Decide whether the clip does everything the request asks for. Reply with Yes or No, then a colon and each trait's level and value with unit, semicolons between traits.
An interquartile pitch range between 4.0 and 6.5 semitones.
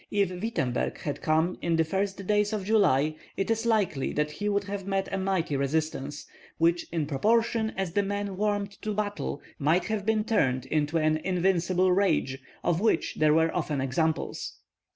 Yes: average, 4.6 semitones